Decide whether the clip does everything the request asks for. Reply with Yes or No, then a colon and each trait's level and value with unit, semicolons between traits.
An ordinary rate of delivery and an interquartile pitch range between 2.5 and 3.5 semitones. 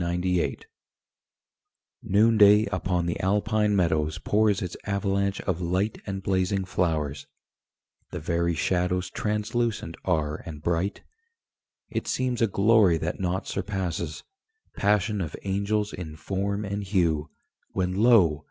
No: slow, 120 wpm; average, 3.2 semitones